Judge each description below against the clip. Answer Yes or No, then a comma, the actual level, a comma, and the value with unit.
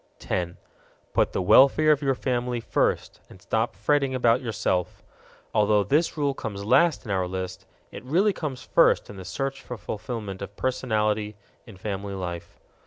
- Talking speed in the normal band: Yes, average, 165 wpm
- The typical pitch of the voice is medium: No, low, 110 Hz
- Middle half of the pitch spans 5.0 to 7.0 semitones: Yes, average, 5.3 semitones